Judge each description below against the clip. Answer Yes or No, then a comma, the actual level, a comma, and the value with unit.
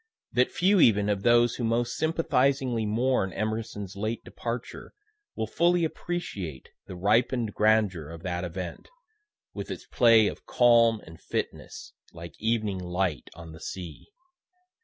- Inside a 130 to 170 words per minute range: Yes, average, 140 wpm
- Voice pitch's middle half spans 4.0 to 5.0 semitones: Yes, average, 4.6 semitones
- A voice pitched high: No, low, 110 Hz